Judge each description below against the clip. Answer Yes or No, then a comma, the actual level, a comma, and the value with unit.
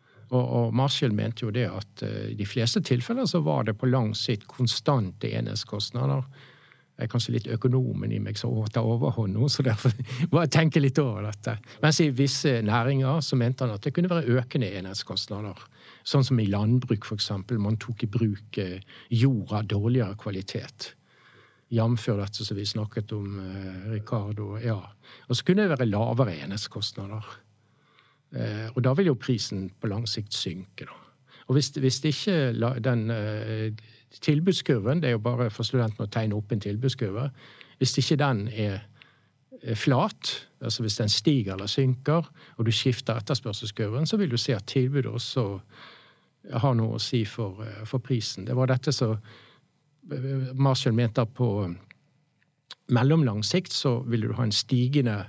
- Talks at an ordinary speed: Yes, average, 165 wpm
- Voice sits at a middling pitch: No, low, 120 Hz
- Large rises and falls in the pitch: No, average, 3.6 semitones